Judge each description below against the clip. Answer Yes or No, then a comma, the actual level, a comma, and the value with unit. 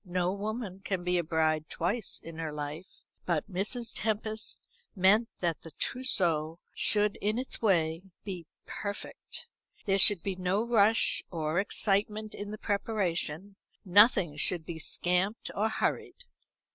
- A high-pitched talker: Yes, high, 195 Hz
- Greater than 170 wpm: No, average, 140 wpm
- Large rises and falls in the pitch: No, average, 4.0 semitones